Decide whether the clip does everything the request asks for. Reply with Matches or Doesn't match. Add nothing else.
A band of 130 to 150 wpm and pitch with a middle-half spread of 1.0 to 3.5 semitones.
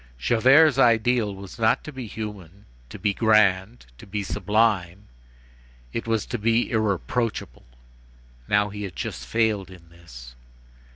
Matches